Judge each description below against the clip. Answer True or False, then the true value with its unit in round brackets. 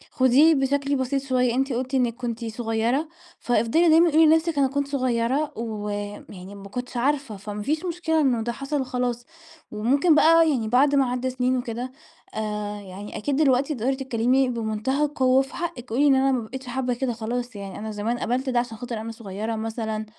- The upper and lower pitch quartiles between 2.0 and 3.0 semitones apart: False (3.5 semitones)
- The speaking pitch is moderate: False (250 Hz)